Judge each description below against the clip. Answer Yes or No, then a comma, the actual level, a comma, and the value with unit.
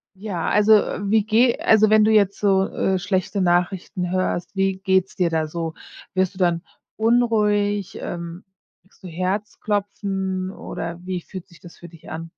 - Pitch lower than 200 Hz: Yes, high, 190 Hz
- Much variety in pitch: No, average, 2.8 semitones